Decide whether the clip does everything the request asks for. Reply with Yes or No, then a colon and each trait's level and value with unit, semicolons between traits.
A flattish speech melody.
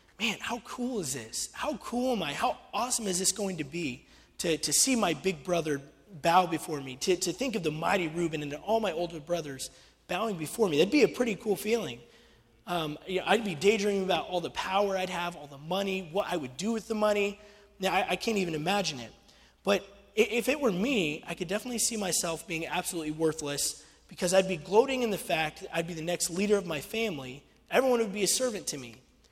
No: average, 4.6 semitones